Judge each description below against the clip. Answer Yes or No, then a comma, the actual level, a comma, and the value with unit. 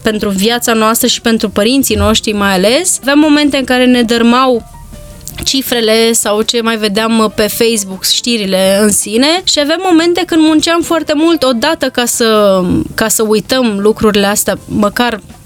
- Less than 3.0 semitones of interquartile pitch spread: No, average, 3.8 semitones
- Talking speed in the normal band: Yes, average, 160 wpm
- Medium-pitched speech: No, high, 230 Hz